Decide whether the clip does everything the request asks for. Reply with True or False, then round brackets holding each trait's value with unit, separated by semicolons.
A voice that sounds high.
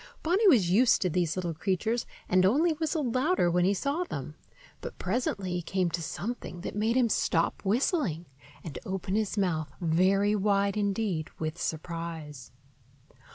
True (195 Hz)